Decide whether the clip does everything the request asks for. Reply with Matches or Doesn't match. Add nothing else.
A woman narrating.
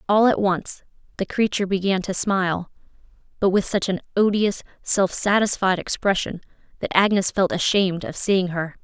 Matches